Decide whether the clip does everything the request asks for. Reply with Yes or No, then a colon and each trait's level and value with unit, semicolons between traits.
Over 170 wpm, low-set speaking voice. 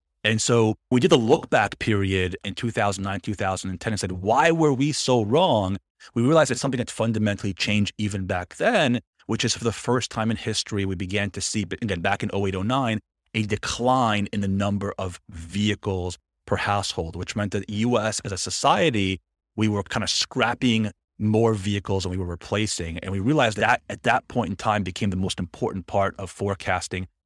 Yes: average, 195 wpm; low, 100 Hz